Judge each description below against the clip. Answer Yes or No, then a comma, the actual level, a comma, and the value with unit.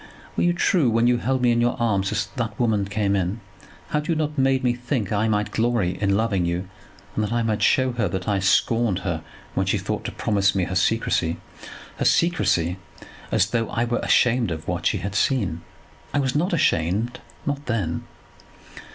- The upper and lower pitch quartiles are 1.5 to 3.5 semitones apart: No, average, 4.1 semitones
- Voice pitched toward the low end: Yes, low, 110 Hz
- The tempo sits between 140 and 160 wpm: No, fast, 205 wpm